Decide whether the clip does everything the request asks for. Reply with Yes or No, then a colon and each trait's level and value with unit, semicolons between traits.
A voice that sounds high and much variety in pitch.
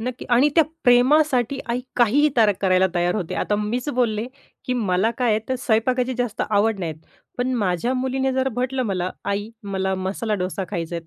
No: high, 225 Hz; average, 4.8 semitones